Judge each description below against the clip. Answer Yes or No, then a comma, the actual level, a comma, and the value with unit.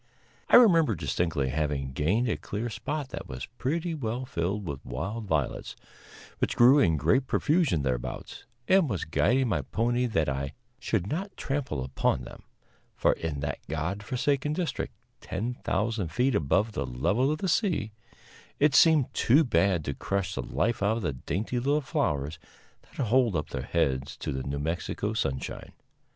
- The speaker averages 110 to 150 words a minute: No, average, 165 wpm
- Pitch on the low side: Yes, low, 105 Hz